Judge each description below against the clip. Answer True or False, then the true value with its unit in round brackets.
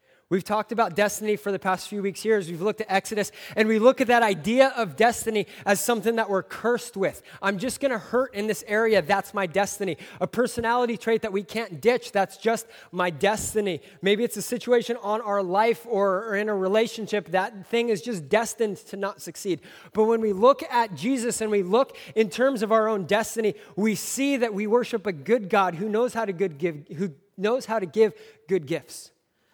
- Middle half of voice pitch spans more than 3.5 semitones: False (2.6 semitones)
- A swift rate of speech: True (215 wpm)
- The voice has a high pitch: True (215 Hz)